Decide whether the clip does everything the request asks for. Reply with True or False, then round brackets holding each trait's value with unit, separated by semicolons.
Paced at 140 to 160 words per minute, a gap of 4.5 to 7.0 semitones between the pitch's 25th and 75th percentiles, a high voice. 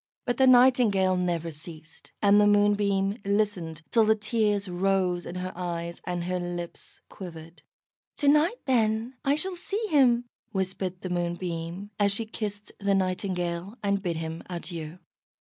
False (150 wpm; 3.6 semitones; 195 Hz)